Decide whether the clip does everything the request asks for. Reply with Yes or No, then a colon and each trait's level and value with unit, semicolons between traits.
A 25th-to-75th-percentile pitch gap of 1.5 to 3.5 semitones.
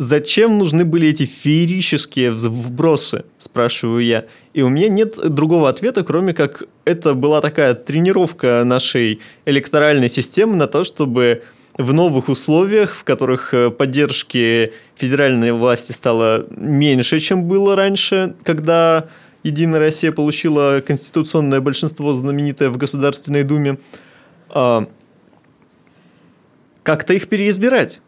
No: average, 4.0 semitones